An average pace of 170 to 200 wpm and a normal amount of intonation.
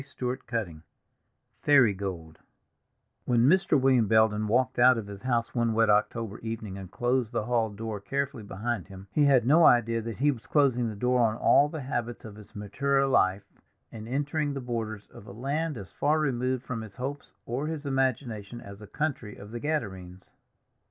Yes: average, 185 wpm; average, 4.2 semitones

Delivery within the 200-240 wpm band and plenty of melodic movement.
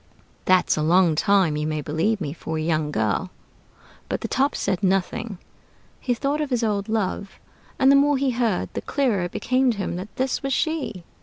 Yes: fast, 205 wpm; wide, 7.0 semitones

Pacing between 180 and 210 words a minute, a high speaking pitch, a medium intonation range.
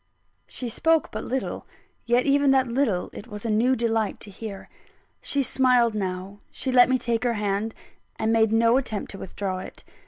Yes: average, 185 wpm; high, 230 Hz; average, 3.5 semitones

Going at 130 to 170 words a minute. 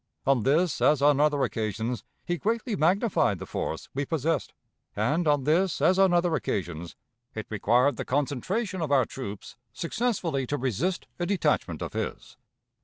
Yes: average, 160 wpm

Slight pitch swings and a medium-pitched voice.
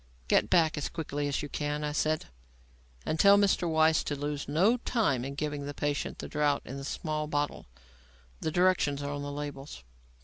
Yes: narrow, 1.7 semitones; medium, 150 Hz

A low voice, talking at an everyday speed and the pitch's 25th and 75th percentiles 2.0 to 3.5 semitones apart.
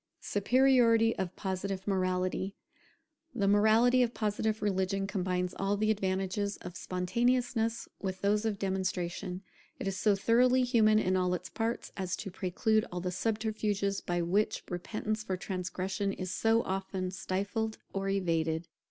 No: high, 195 Hz; average, 145 wpm; average, 2.8 semitones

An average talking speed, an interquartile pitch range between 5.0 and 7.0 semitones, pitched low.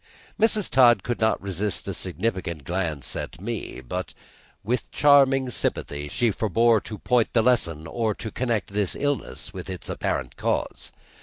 Yes: average, 155 wpm; wide, 5.4 semitones; low, 110 Hz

